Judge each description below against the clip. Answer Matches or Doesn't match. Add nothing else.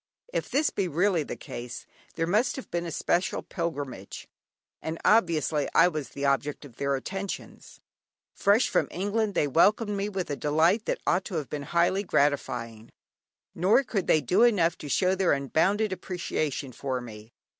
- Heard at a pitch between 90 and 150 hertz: Doesn't match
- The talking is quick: Doesn't match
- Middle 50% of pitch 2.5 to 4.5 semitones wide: Doesn't match